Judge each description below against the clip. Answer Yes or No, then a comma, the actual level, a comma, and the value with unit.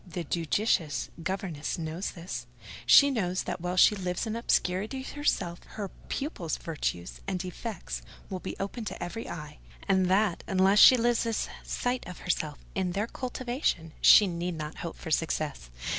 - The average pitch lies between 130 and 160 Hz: No, medium, 185 Hz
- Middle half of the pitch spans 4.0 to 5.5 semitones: Yes, average, 4.6 semitones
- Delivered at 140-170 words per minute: Yes, average, 160 wpm